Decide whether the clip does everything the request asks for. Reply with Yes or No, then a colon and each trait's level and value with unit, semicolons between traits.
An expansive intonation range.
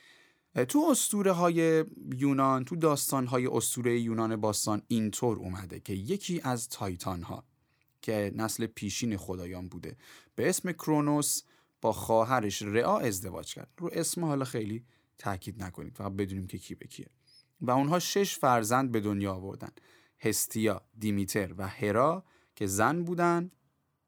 Yes: wide, 7.1 semitones